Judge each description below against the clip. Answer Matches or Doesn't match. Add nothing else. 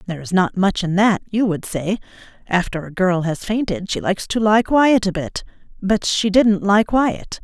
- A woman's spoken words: Matches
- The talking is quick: Matches